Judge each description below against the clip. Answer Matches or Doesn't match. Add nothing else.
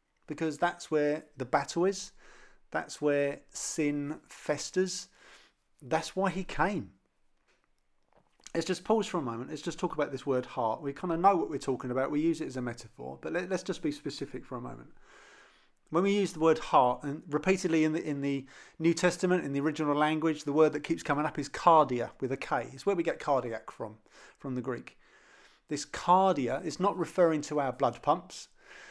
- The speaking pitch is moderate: Matches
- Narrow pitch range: Doesn't match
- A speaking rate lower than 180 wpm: Doesn't match